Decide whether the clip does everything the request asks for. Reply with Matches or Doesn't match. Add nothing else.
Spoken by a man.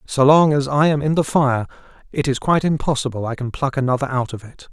Matches